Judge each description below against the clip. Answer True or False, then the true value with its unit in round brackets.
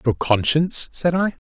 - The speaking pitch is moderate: True (155 Hz)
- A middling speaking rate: True (160 wpm)